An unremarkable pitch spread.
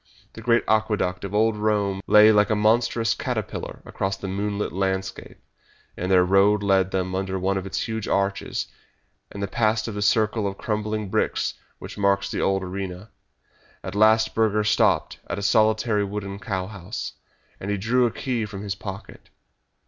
No: narrow, 1.9 semitones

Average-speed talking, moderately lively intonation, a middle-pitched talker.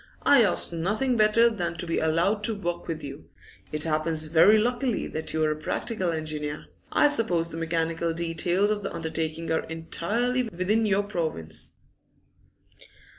Yes: average, 160 wpm; average, 4.9 semitones; medium, 170 Hz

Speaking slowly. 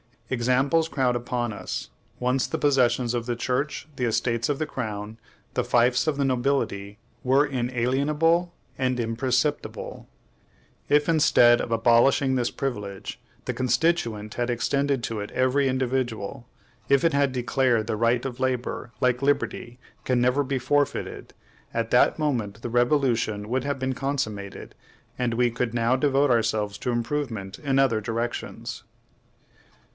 No: average, 145 wpm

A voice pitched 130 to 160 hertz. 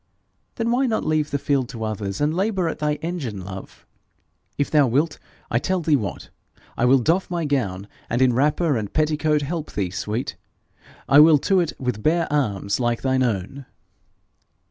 Yes: medium, 140 Hz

